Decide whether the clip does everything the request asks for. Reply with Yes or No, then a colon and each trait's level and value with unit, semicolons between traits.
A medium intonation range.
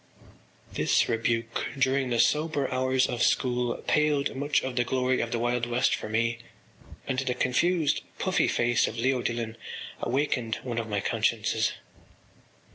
No: narrow, 2.2 semitones